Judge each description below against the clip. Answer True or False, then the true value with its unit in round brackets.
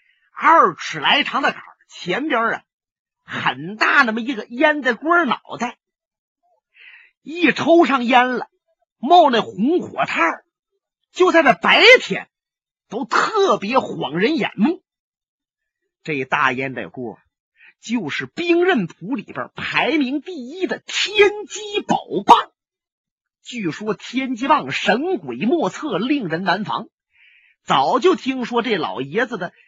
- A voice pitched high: True (295 Hz)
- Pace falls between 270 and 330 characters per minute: False (175 characters per minute)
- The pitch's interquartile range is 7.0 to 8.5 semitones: True (7.7 semitones)